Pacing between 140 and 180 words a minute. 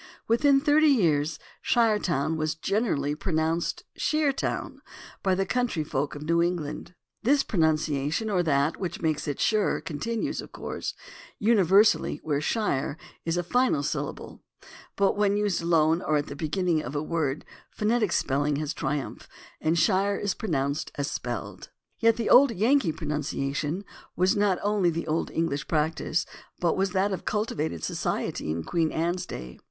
Yes: average, 160 wpm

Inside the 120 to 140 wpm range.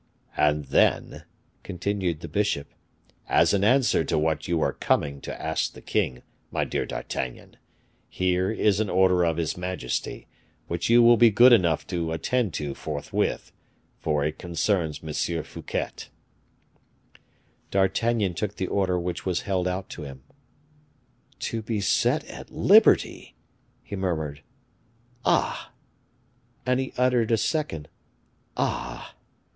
Yes: slow, 135 wpm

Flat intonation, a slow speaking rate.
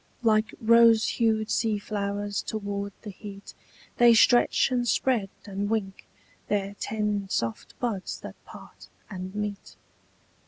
Yes: narrow, 1.9 semitones; slow, 125 wpm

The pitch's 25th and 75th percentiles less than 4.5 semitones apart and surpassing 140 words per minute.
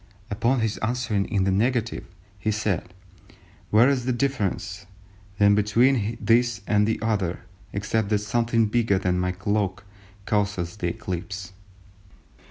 No: average, 2.7 semitones; slow, 135 wpm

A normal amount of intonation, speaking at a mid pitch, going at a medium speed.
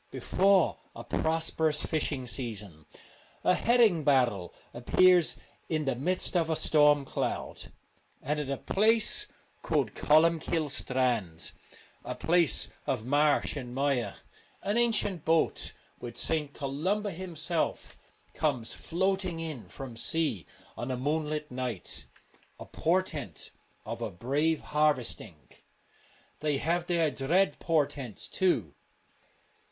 No: average, 4.7 semitones; medium, 150 Hz; slow, 125 wpm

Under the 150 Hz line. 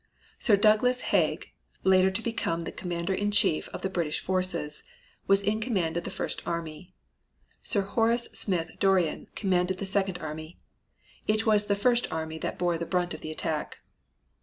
No: medium, 185 Hz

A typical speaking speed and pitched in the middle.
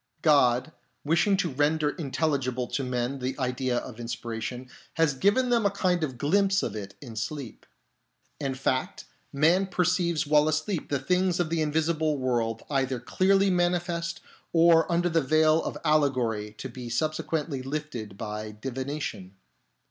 Yes: average, 150 wpm; medium, 150 Hz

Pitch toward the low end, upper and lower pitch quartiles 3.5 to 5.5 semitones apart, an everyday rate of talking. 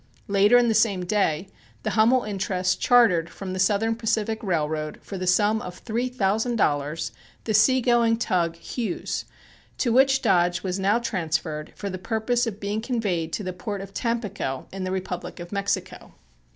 No: high, 200 Hz; average, 3.9 semitones; average, 175 wpm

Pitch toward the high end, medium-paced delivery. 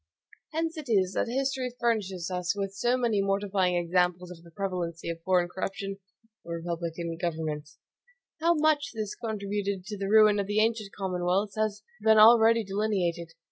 Yes: high, 195 Hz; average, 160 wpm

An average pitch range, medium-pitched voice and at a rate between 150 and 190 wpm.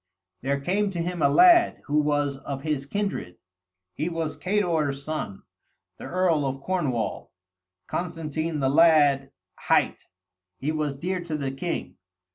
No: average, 3.9 semitones; medium, 155 Hz; average, 140 wpm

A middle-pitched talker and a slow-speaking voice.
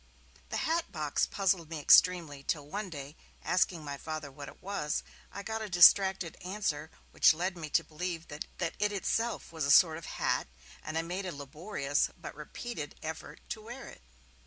No: medium, 165 Hz; average, 185 wpm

